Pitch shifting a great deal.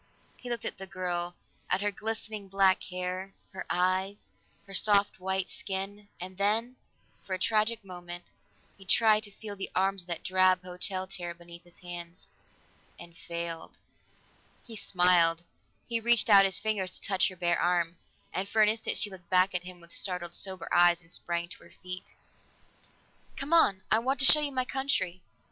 No: average, 2.7 semitones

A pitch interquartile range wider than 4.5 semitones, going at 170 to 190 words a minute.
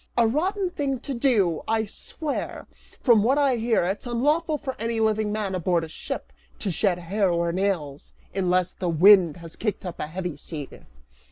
Yes: wide, 5.4 semitones; average, 175 wpm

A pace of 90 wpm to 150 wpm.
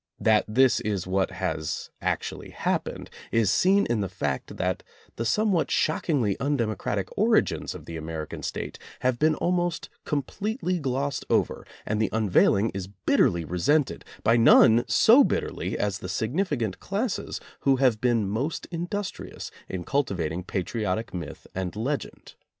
Yes: average, 145 wpm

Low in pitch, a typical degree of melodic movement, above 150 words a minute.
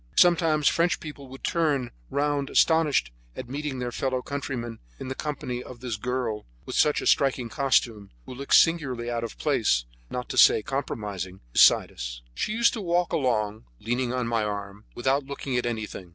Yes: low, 125 Hz; average, 4.0 semitones; average, 175 wpm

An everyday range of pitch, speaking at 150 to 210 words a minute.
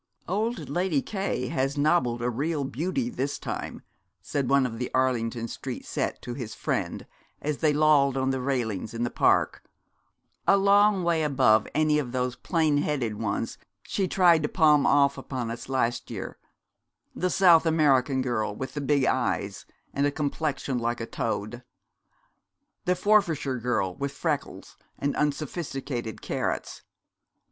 Yes: average, 4.1 semitones; average, 155 wpm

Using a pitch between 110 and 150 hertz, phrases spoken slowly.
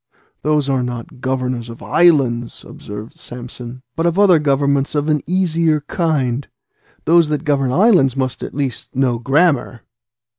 No: medium, 140 Hz; average, 145 wpm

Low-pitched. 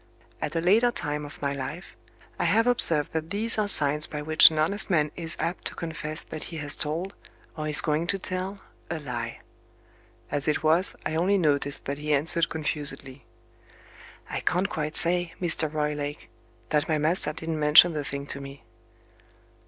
No: medium, 155 Hz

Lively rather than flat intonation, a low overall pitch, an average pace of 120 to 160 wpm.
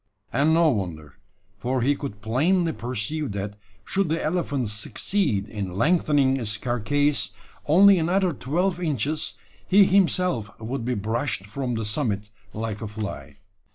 Yes: wide, 7.2 semitones; low, 130 Hz; average, 140 wpm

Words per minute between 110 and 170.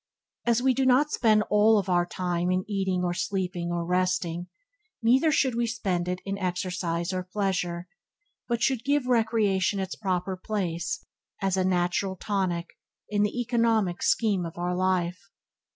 Yes: average, 155 wpm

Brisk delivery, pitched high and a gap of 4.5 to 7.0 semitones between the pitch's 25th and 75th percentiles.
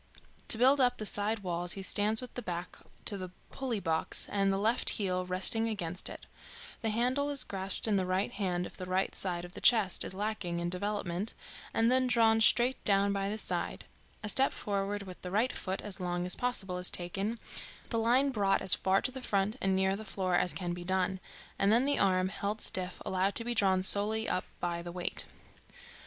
No: fast, 215 wpm; high, 195 Hz; average, 3.3 semitones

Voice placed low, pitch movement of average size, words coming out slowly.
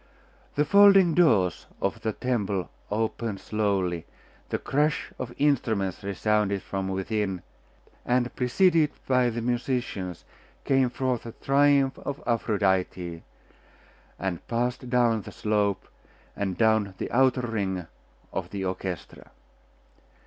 Yes: low, 110 Hz; average, 4.8 semitones; slow, 115 wpm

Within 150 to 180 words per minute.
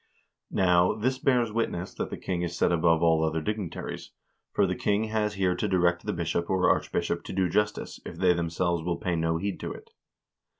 No: fast, 205 wpm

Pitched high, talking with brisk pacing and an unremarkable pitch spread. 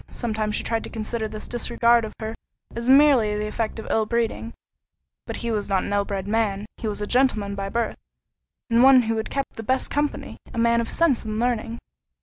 No: high, 225 Hz; fast, 210 wpm; narrow, 1.9 semitones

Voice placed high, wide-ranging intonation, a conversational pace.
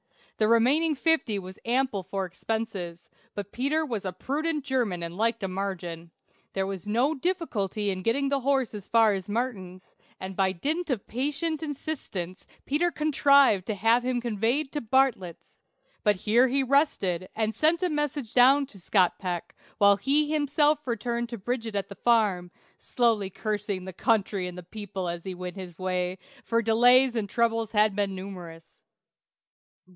Yes: high, 225 Hz; wide, 5.9 semitones; average, 170 wpm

